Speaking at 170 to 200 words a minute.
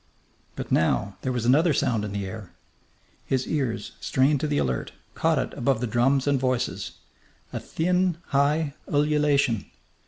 No: average, 155 wpm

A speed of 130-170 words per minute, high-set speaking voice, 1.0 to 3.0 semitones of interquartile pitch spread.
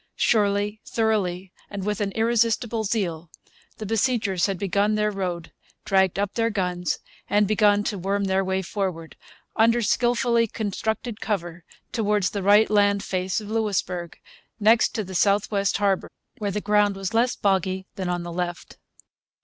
Yes: average, 155 wpm; high, 205 Hz; narrow, 2.4 semitones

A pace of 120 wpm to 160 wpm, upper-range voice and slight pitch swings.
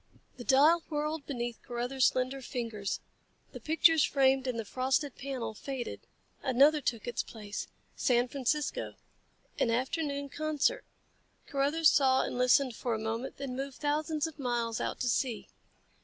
No: average, 145 wpm; very high, 265 Hz; average, 3.2 semitones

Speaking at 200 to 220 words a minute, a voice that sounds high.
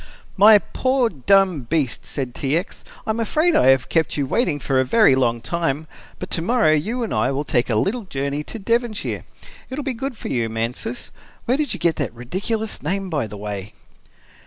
No: fast, 205 wpm; medium, 165 Hz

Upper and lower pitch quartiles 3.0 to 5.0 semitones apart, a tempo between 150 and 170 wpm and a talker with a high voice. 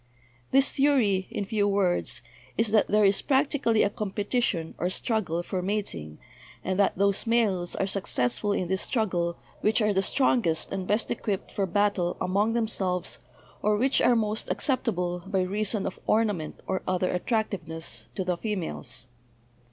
Yes: average, 3.3 semitones; average, 160 wpm; high, 200 Hz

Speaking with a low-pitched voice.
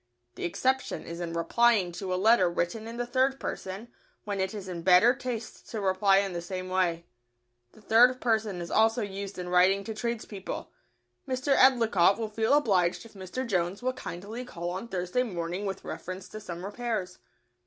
No: high, 200 Hz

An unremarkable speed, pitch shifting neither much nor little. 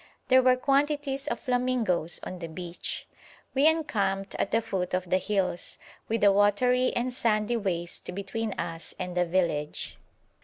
No: average, 155 wpm; wide, 5.7 semitones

